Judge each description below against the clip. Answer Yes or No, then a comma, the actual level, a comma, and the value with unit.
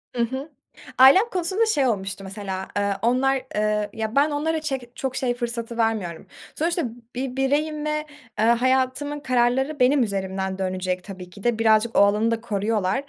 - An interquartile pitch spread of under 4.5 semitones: No, average, 4.8 semitones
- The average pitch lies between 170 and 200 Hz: No, high, 240 Hz